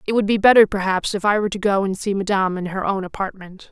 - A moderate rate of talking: No, fast, 275 wpm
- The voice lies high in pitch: Yes, high, 200 Hz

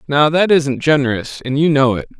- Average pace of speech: No, fast, 220 wpm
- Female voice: No, male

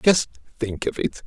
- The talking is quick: No, average, 190 wpm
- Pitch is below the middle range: Yes, low, 130 Hz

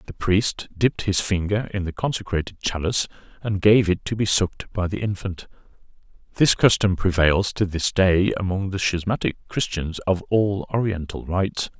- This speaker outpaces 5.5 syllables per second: No, 5.0 syllables/s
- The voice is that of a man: Yes, male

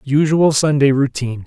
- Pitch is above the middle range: No, medium, 140 Hz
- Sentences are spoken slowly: Yes, slow, 125 wpm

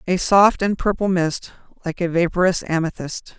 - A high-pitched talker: No, medium, 180 Hz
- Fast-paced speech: No, average, 160 wpm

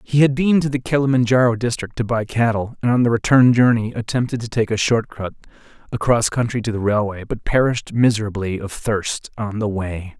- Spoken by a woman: No, male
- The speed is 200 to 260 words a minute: Yes, fast, 205 wpm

